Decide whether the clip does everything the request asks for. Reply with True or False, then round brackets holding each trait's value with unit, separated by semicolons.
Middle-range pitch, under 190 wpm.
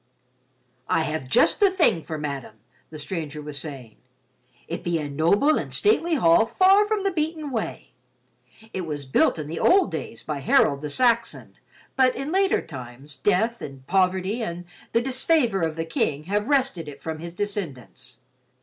True (170 Hz; 170 wpm)